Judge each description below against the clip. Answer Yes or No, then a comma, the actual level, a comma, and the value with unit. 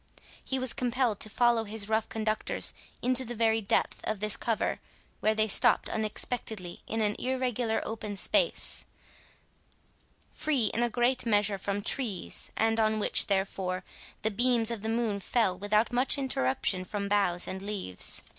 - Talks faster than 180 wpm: No, average, 155 wpm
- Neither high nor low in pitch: No, high, 220 Hz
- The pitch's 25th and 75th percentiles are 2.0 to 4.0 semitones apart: Yes, average, 2.8 semitones